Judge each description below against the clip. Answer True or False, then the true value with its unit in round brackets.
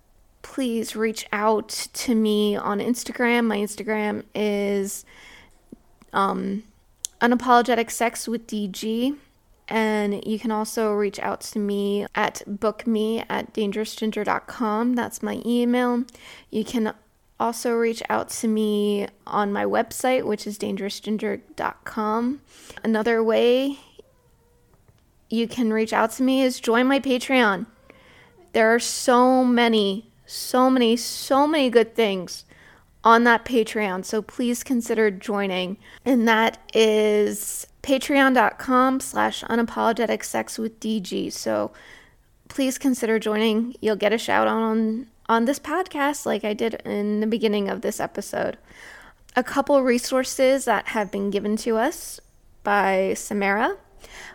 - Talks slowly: True (120 wpm)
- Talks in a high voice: True (225 Hz)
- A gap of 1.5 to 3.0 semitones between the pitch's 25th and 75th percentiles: True (2.5 semitones)